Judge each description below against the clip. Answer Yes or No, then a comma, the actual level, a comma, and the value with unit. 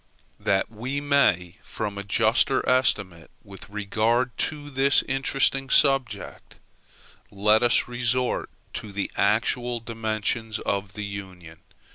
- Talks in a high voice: No, low, 110 Hz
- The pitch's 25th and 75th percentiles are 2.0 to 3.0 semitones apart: No, average, 4.2 semitones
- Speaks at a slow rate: Yes, slow, 115 wpm